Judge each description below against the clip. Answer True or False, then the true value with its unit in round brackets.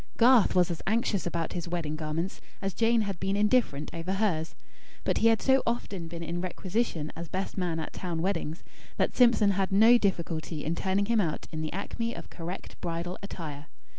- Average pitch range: True (3.9 semitones)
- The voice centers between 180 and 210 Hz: True (185 Hz)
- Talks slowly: False (195 wpm)